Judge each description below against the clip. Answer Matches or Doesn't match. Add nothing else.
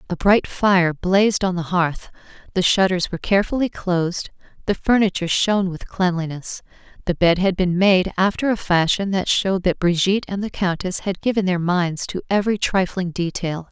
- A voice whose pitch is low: Doesn't match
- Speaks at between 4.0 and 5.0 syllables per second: Doesn't match